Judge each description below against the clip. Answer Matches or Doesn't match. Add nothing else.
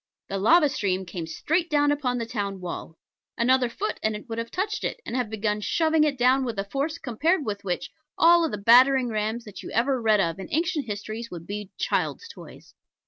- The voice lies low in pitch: Doesn't match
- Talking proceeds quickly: Matches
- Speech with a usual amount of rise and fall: Doesn't match